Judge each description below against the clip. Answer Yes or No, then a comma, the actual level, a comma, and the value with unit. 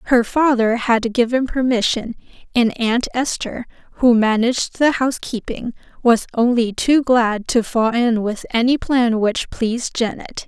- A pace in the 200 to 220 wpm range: No, average, 145 wpm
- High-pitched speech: Yes, high, 240 Hz